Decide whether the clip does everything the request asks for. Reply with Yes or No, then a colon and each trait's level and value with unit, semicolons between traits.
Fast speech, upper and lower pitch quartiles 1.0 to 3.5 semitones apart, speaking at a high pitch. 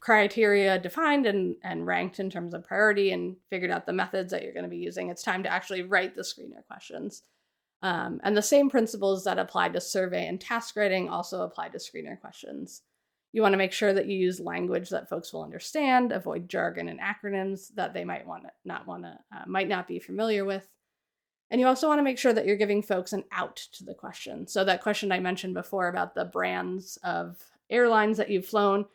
Yes: fast, 220 wpm; narrow, 2.5 semitones; high, 195 Hz